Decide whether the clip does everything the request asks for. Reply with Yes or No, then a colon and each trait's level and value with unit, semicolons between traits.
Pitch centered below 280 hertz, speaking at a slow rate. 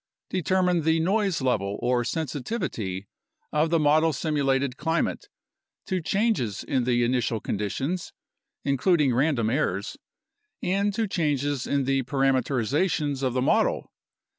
Yes: medium, 140 Hz; slow, 120 wpm